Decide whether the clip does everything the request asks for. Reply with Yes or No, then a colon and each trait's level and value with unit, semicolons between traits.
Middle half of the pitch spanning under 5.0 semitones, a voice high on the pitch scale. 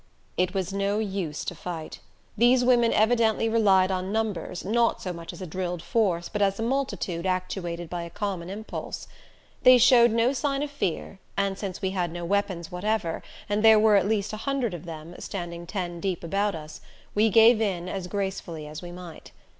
Yes: average, 4.0 semitones; high, 195 Hz